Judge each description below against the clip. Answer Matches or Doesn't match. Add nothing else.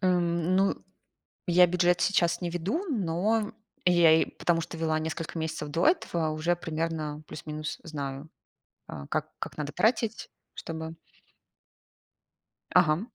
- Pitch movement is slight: Matches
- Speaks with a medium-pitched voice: Matches